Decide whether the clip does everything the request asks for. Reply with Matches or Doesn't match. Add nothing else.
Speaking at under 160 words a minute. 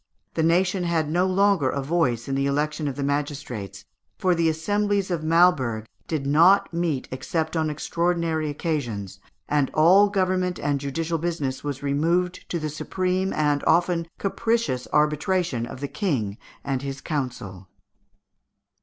Matches